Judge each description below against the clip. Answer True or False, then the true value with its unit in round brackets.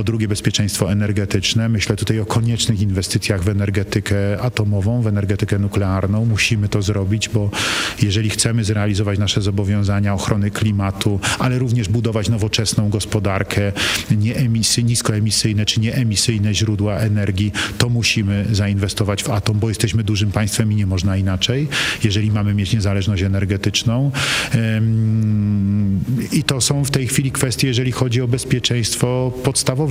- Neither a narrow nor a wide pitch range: False (2.2 semitones)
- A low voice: True (110 Hz)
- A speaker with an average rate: True (135 wpm)